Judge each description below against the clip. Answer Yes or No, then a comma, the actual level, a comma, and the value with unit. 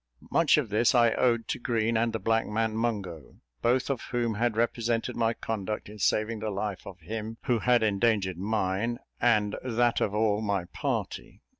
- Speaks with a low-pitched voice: Yes, low, 110 Hz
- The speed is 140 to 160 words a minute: No, average, 180 wpm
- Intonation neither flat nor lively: No, narrow, 2.1 semitones